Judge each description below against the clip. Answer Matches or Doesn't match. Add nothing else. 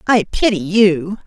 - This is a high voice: Matches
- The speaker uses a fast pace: Doesn't match